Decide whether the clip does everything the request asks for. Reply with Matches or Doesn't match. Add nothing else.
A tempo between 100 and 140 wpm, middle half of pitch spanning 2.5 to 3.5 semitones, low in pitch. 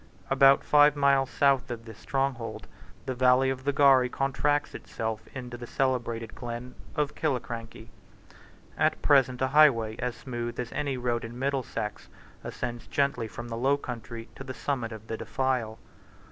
Doesn't match